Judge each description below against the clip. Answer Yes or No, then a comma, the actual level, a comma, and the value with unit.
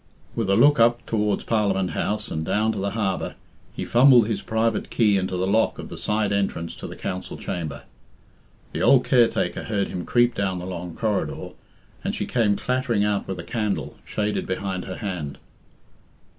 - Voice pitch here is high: No, low, 105 Hz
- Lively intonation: No, average, 3.3 semitones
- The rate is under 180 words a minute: No, average, 185 wpm